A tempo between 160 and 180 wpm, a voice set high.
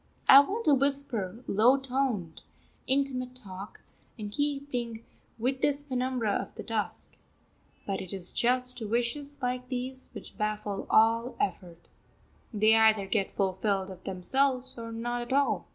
No: average, 140 wpm; high, 240 Hz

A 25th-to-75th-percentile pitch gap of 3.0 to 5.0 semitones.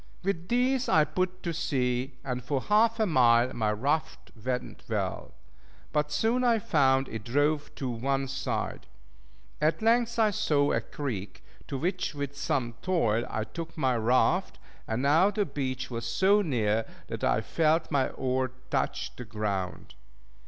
No: wide, 5.6 semitones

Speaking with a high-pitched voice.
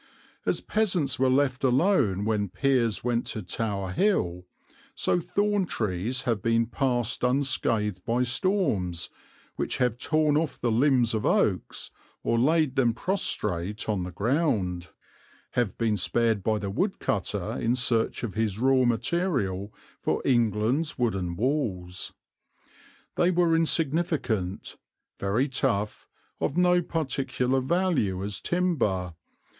No: low, 120 Hz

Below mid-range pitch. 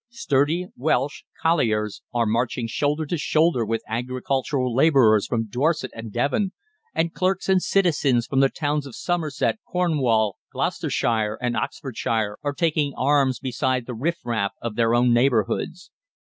Yes: low, 130 Hz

